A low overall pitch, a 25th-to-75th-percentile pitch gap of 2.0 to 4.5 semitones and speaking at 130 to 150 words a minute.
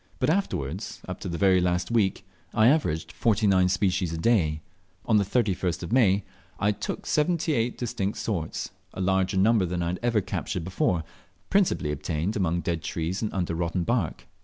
No: very low, 95 Hz; average, 4.2 semitones; average, 175 wpm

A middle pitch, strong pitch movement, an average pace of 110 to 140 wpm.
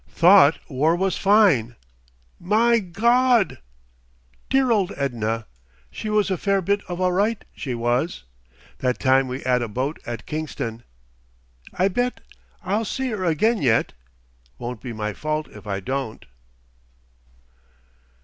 Yes: medium, 165 Hz; wide, 8.5 semitones; slow, 135 wpm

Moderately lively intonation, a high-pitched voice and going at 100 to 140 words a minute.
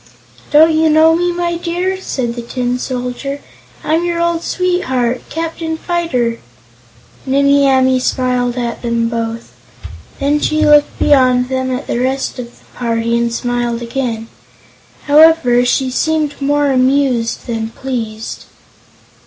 Yes: average, 4.4 semitones; very high, 260 Hz; slow, 135 wpm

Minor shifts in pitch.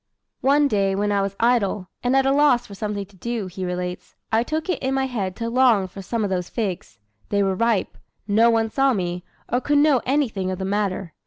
No: average, 4.7 semitones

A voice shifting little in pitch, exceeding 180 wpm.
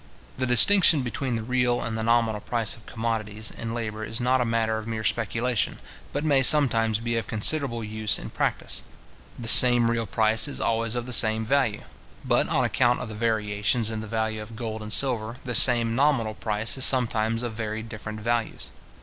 Yes: narrow, 1.9 semitones; average, 195 wpm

